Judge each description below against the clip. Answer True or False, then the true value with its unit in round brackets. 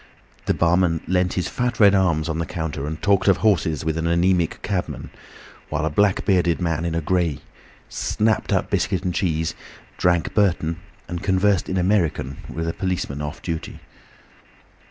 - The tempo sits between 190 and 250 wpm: False (165 wpm)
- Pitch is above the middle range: False (85 Hz)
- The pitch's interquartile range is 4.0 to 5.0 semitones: False (2.6 semitones)